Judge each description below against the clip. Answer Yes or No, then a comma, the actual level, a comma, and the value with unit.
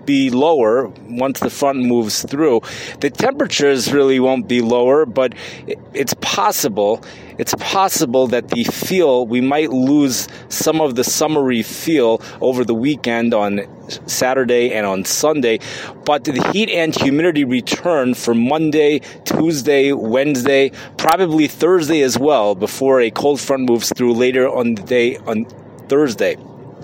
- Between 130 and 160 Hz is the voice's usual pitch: Yes, low, 135 Hz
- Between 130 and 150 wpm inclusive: Yes, average, 140 wpm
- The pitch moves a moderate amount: Yes, average, 3.9 semitones